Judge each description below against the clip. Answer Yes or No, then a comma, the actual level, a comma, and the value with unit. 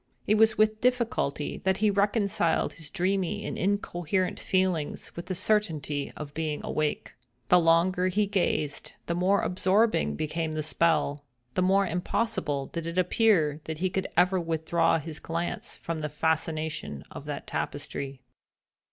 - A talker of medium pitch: Yes, medium, 170 Hz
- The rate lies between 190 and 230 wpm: No, average, 145 wpm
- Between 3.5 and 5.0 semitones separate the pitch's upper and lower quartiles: Yes, average, 3.9 semitones